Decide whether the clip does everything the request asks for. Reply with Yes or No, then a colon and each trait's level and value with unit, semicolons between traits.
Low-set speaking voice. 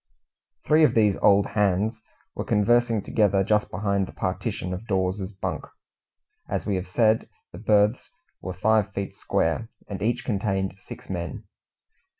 Yes: low, 100 Hz